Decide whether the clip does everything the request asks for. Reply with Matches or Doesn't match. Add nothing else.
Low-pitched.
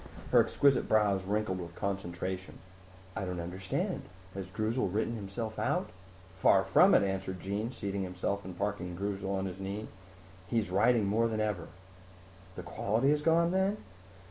Matches